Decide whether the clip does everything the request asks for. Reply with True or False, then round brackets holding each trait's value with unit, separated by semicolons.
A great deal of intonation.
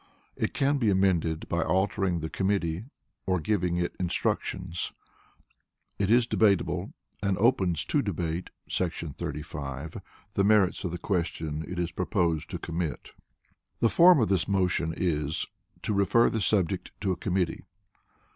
False (3.2 semitones)